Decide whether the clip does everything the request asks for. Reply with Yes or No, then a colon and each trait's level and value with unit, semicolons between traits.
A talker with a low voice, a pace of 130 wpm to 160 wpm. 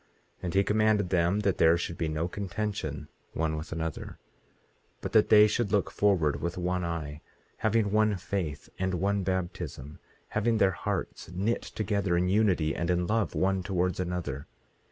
No: very low, 90 Hz; average, 170 wpm